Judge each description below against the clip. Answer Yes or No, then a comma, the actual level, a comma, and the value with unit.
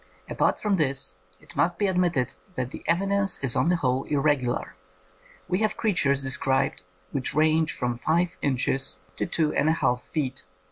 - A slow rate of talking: No, average, 175 wpm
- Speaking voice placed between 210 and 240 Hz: No, medium, 145 Hz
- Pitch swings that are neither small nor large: Yes, average, 4.7 semitones